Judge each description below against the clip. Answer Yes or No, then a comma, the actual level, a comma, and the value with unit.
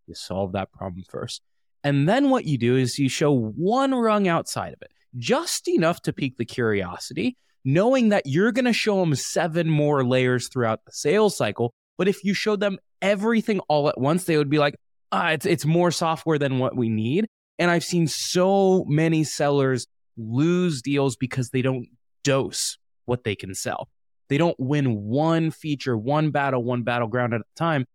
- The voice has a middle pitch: Yes, medium, 145 Hz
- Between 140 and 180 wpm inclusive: No, average, 190 wpm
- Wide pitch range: Yes, wide, 6.1 semitones